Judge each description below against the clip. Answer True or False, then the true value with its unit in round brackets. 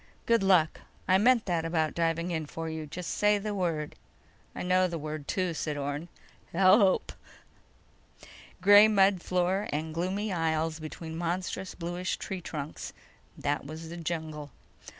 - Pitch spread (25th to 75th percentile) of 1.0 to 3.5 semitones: True (2.9 semitones)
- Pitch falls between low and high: True (170 Hz)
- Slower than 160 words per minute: True (145 wpm)